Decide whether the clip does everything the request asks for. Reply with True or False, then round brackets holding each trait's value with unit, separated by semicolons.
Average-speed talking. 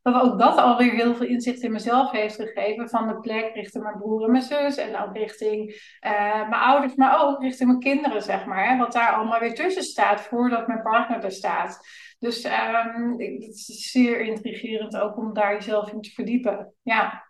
False (210 wpm)